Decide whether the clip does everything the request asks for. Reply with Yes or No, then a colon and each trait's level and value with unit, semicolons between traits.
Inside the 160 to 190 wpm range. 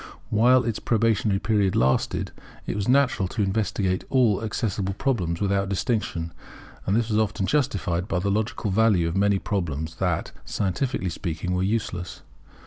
No: average, 150 wpm